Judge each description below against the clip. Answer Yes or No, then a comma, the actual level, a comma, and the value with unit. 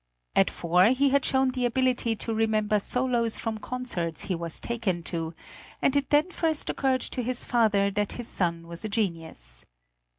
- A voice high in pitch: Yes, high, 225 Hz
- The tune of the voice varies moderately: No, wide, 6.1 semitones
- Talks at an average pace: Yes, average, 175 wpm